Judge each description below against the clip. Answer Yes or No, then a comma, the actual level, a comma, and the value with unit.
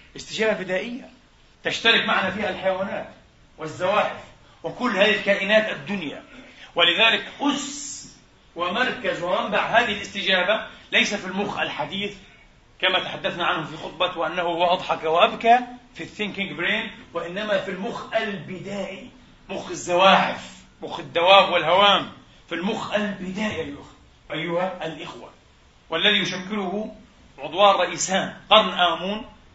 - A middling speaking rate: Yes, average, 105 wpm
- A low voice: No, high, 200 Hz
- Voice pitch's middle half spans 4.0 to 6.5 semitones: No, average, 3.3 semitones